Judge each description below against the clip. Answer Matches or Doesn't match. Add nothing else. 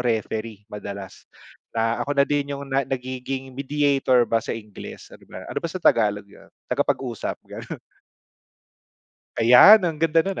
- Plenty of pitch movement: Doesn't match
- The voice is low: Matches